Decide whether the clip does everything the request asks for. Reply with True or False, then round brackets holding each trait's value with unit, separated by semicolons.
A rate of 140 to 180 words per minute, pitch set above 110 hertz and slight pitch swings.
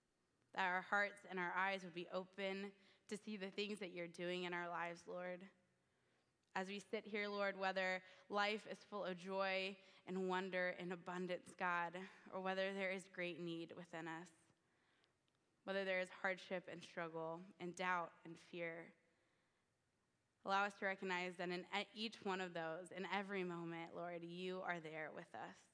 True (170 wpm; 185 Hz; 1.8 semitones)